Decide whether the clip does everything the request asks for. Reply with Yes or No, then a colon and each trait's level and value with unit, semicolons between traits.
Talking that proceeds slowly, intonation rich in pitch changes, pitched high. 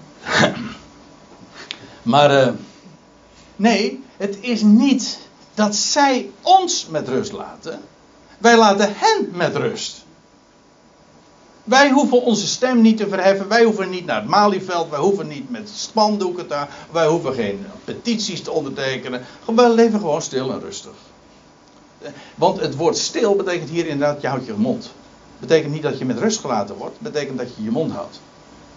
No: average, 150 wpm; wide, 6.4 semitones; high, 205 Hz